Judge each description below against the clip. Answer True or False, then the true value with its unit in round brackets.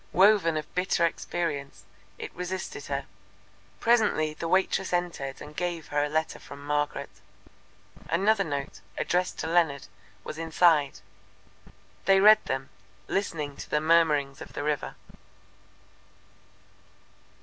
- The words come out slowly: True (120 wpm)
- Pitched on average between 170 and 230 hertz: False (160 Hz)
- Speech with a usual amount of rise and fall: True (3.6 semitones)